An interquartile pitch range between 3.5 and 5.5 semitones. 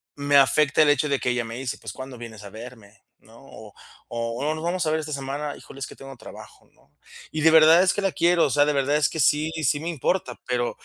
Yes: average, 3.9 semitones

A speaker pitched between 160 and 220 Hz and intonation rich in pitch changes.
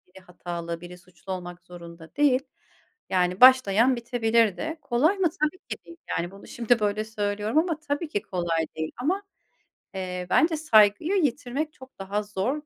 Yes: high, 215 Hz; wide, 7.9 semitones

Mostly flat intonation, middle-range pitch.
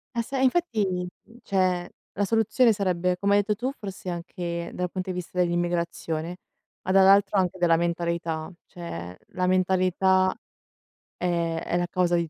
Yes: narrow, 2.1 semitones; medium, 180 Hz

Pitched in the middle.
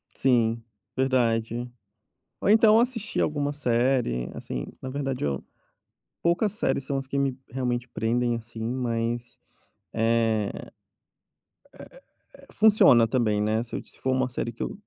No: low, 125 Hz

